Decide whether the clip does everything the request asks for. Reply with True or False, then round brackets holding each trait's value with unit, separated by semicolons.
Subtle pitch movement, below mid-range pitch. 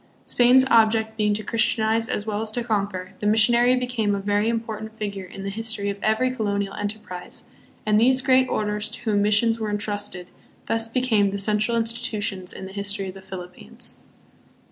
False (2.1 semitones; 215 Hz)